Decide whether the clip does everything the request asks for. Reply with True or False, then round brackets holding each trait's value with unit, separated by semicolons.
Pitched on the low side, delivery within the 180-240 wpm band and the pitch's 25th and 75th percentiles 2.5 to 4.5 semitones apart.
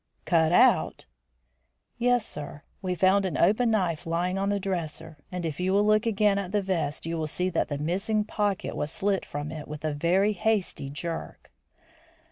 False (180 Hz; 185 wpm; 4.1 semitones)